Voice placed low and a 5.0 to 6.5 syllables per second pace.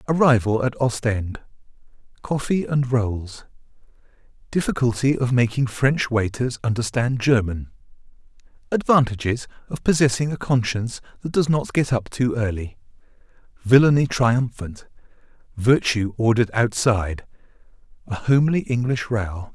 No: low, 120 Hz; 4.8 syllables/s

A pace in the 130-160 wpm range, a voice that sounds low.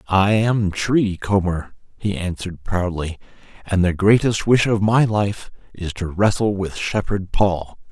Yes: average, 150 wpm; low, 100 Hz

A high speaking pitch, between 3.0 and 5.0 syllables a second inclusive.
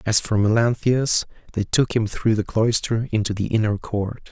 No: low, 110 Hz; 4.6 syllables/s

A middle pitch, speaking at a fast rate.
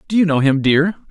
Yes: medium, 160 Hz; fast, 270 wpm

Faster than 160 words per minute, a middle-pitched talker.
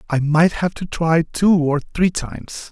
Yes: average, 200 wpm; medium, 165 Hz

